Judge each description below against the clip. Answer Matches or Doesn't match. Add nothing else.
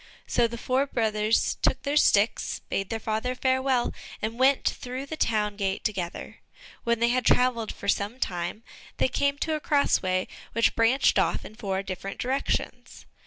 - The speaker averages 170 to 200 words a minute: Matches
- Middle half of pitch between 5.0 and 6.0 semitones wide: Doesn't match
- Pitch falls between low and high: Doesn't match